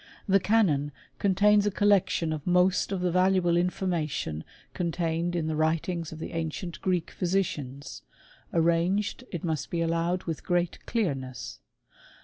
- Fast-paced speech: No, average, 140 wpm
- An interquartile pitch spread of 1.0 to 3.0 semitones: Yes, average, 2.7 semitones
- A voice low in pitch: No, medium, 175 Hz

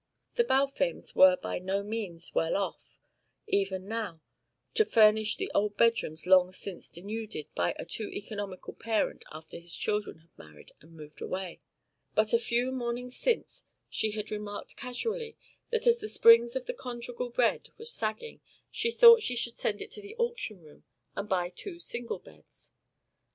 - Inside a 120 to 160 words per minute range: No, average, 170 wpm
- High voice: Yes, high, 220 Hz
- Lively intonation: Yes, wide, 6.4 semitones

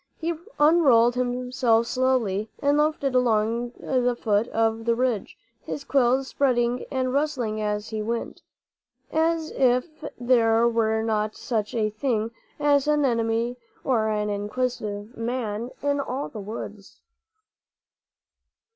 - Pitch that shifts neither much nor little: Yes, average, 3.0 semitones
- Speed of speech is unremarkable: No, slow, 125 wpm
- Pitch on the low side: No, high, 240 Hz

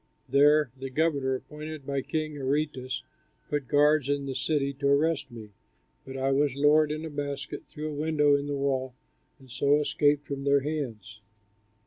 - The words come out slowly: No, average, 170 wpm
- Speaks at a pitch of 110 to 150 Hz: Yes, medium, 140 Hz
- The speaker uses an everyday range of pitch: No, narrow, 1.9 semitones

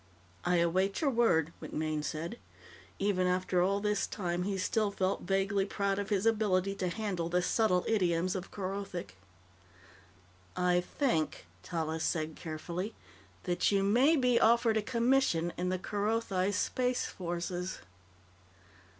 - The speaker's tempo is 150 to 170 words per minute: No, slow, 135 wpm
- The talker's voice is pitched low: No, high, 190 Hz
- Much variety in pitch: No, average, 3.1 semitones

